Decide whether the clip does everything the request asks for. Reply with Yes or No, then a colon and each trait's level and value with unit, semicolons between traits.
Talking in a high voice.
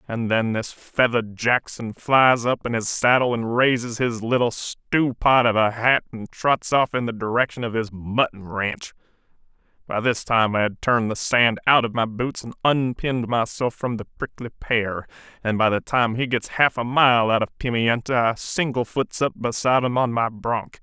No: low, 120 Hz